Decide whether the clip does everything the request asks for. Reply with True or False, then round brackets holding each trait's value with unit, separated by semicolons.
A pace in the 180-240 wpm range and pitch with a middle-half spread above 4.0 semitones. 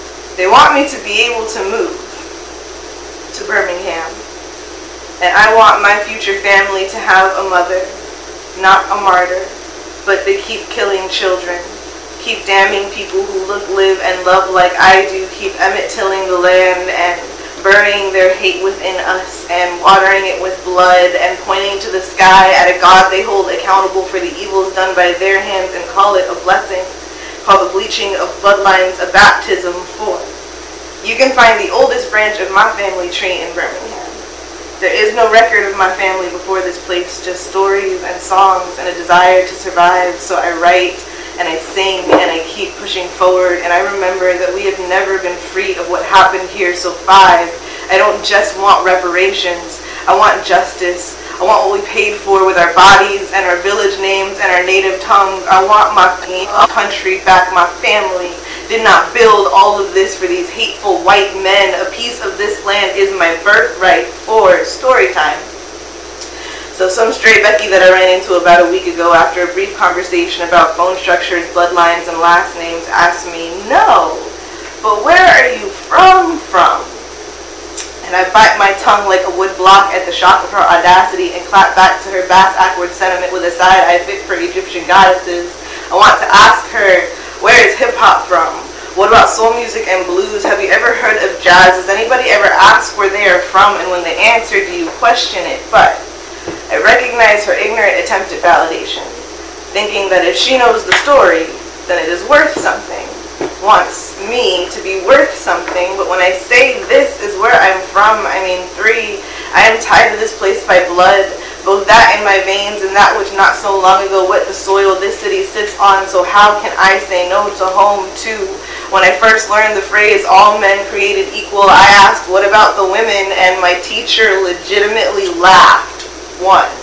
False (185 wpm; 3.2 semitones)